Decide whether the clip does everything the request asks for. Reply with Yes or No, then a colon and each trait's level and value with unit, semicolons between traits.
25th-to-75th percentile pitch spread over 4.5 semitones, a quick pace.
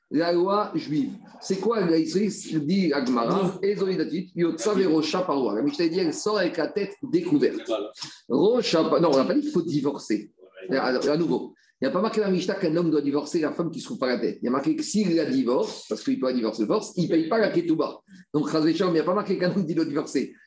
Yes: average, 4.9 semitones; fast, 275 wpm